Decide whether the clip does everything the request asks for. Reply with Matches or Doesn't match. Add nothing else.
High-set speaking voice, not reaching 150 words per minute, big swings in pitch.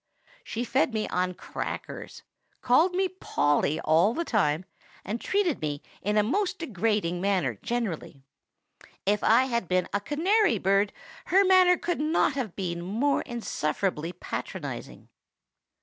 Matches